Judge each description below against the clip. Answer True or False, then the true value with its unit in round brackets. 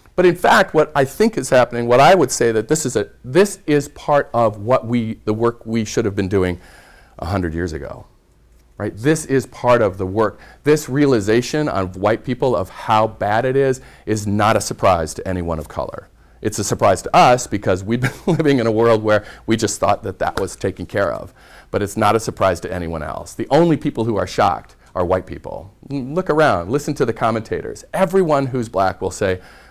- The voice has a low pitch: True (115 Hz)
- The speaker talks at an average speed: False (220 wpm)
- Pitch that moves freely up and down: True (5.7 semitones)